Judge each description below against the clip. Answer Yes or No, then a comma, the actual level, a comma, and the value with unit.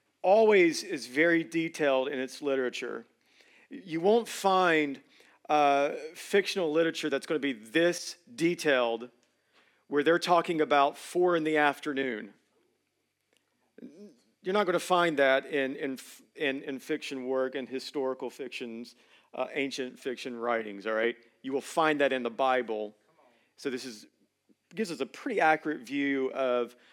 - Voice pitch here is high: No, medium, 140 Hz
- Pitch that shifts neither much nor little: Yes, average, 4.4 semitones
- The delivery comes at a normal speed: Yes, average, 145 wpm